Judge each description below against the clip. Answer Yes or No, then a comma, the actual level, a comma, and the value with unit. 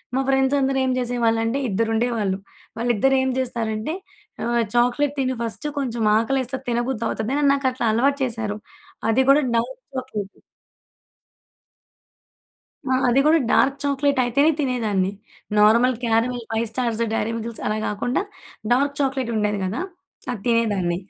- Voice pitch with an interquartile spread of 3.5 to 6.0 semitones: No, average, 2.9 semitones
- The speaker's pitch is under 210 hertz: No, high, 240 Hz